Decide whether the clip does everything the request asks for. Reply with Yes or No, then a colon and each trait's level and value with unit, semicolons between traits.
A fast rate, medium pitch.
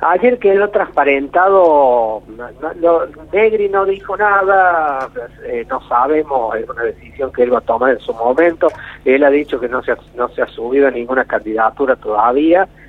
No: average, 180 wpm; medium, 170 Hz